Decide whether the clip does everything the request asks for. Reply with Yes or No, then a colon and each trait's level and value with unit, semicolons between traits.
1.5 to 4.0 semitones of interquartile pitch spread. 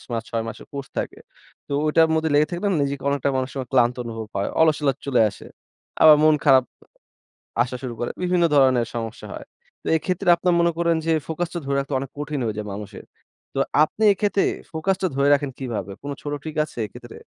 No: average, 4.6 semitones